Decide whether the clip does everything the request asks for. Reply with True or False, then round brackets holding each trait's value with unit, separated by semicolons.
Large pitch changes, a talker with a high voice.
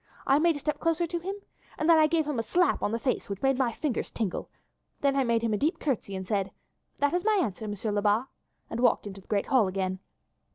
True (7.0 semitones; 255 Hz)